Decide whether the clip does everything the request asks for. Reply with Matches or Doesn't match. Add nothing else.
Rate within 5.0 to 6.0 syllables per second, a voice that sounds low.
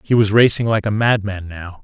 Matches